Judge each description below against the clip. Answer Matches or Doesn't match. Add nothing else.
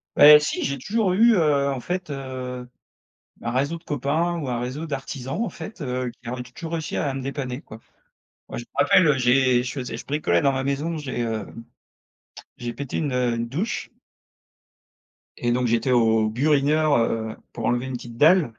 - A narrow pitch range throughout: Doesn't match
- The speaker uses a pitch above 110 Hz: Matches